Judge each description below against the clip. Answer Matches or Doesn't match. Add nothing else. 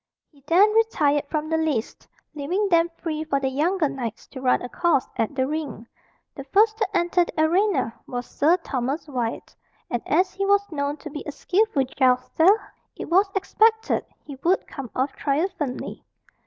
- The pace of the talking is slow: Doesn't match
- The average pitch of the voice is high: Matches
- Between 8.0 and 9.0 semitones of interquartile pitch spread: Doesn't match